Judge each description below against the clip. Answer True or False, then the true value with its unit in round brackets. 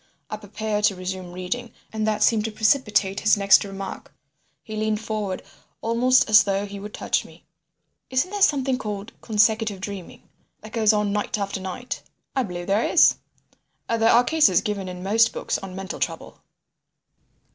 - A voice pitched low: False (210 Hz)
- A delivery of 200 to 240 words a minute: False (165 wpm)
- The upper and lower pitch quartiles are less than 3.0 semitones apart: True (2.5 semitones)